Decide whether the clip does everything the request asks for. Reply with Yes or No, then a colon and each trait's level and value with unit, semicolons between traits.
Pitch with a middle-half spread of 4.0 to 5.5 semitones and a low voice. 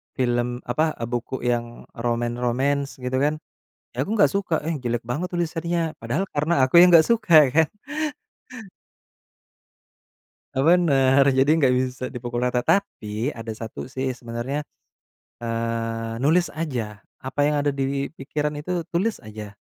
Yes: average, 4.8 semitones; low, 130 Hz